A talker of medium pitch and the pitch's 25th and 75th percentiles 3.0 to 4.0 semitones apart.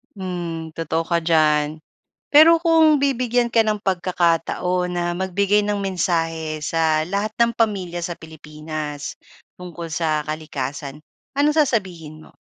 No: medium, 175 Hz; average, 4.7 semitones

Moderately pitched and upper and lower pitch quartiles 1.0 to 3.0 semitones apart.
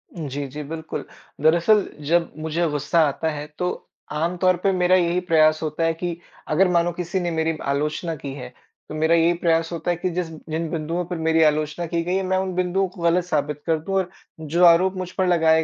Yes: medium, 165 Hz; narrow, 2.4 semitones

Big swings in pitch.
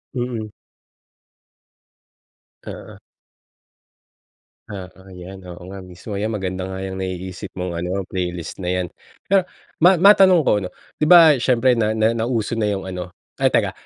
No: average, 4.2 semitones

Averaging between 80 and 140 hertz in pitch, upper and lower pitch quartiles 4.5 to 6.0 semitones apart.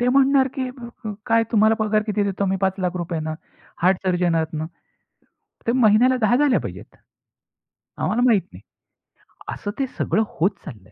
No: high, 210 Hz; average, 5.2 semitones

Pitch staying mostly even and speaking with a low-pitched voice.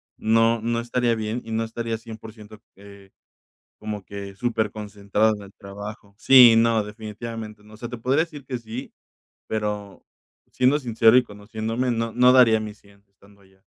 Yes: narrow, 2.1 semitones; low, 110 Hz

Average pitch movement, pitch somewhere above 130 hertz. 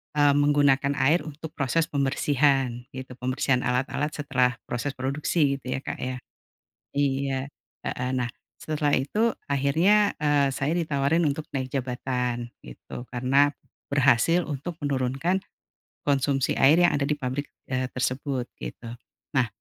No: narrow, 2.3 semitones; medium, 140 Hz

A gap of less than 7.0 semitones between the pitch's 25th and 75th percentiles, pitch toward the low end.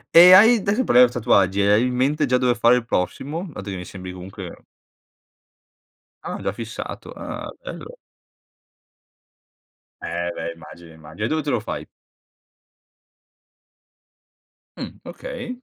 No: wide, 8.1 semitones; low, 120 Hz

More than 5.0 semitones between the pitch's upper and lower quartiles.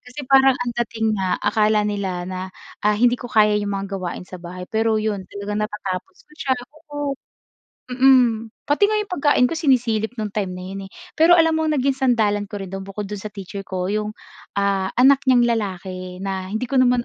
No: average, 4.5 semitones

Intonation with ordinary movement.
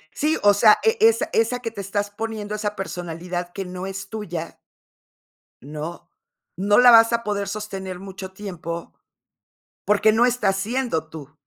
Yes: average, 3.7 semitones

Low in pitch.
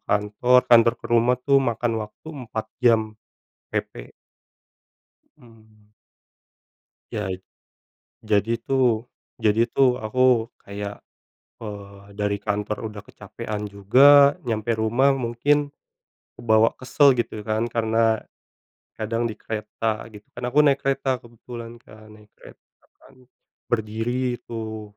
Yes: low, 115 Hz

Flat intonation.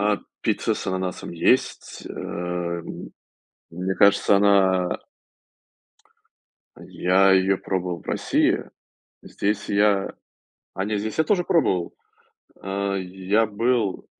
Yes: narrow, 2.0 semitones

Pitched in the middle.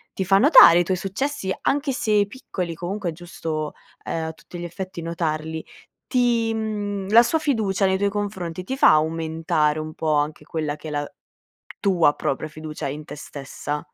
Yes: medium, 175 Hz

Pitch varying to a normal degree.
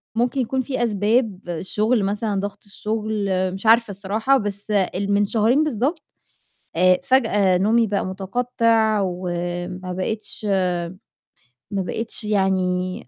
Yes: average, 3.2 semitones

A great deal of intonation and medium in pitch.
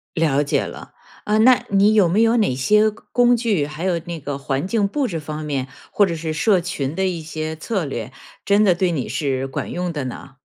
Yes: wide, 5.8 semitones; medium, 170 Hz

